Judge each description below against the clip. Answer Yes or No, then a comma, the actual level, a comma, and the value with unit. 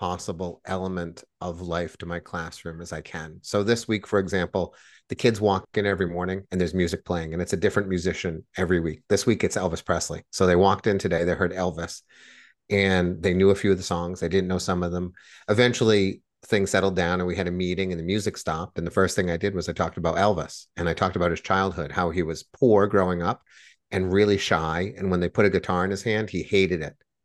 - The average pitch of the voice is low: Yes, very low, 90 Hz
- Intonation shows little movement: Yes, narrow, 2.0 semitones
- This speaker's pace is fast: Yes, fast, 240 wpm